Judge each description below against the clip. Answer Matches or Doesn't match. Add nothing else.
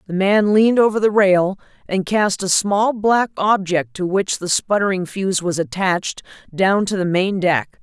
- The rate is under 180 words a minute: Doesn't match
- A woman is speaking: Matches